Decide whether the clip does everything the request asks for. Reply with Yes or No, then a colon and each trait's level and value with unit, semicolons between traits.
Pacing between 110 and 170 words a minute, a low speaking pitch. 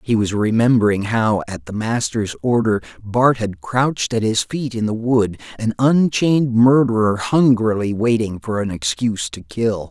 Yes: average, 165 wpm; low, 115 Hz